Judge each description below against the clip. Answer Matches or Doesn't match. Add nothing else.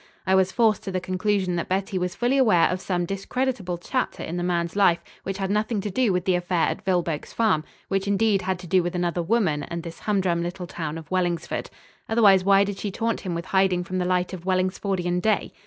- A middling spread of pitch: Doesn't match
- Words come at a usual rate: Doesn't match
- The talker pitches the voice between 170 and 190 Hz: Matches